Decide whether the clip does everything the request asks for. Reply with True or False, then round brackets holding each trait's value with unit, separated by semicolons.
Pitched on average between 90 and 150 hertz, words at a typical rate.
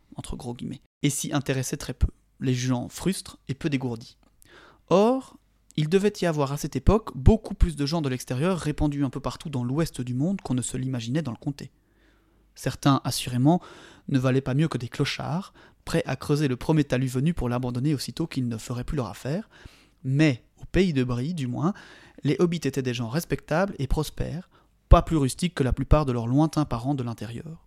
True (140 Hz; 205 wpm)